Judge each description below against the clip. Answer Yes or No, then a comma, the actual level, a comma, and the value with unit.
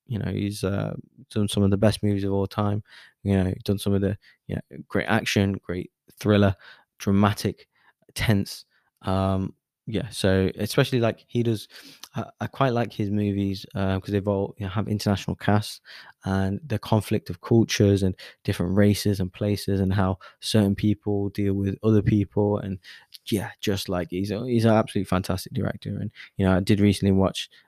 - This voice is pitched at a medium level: No, low, 100 Hz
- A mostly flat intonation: Yes, narrow, 1.6 semitones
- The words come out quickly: No, average, 185 wpm